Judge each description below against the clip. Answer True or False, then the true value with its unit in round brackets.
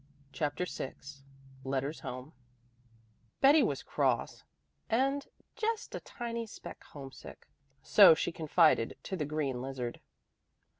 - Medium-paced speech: False (110 wpm)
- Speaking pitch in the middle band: True (155 Hz)